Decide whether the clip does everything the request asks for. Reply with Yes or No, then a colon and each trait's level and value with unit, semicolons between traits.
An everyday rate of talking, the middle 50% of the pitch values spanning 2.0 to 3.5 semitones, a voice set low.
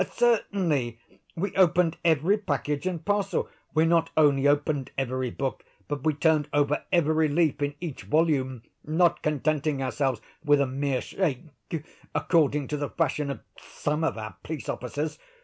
No: average, 150 wpm; average, 2.9 semitones; medium, 150 Hz